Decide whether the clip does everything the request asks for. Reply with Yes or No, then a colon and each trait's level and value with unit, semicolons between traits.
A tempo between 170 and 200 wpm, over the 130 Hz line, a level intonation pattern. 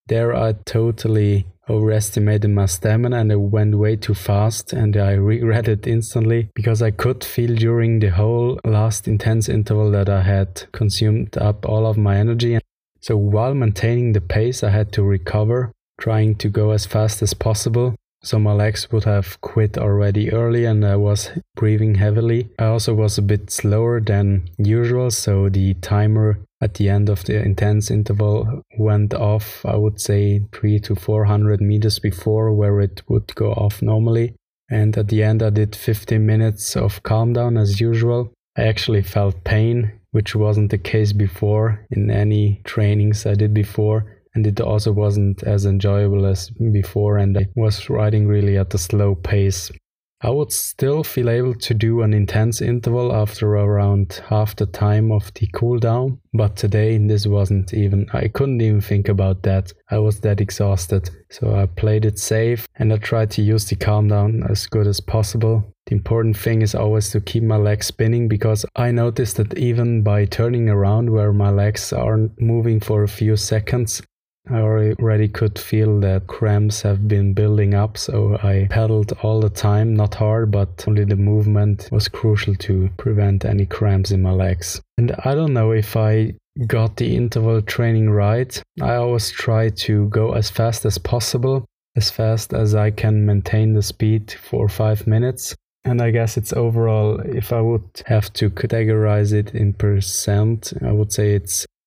No: average, 175 wpm; low, 105 Hz; narrow, 1.6 semitones